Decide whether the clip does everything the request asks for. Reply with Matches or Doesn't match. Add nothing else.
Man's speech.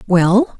Doesn't match